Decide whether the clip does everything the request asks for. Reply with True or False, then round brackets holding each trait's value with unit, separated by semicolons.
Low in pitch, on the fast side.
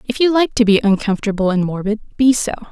False (220 Hz; 220 wpm)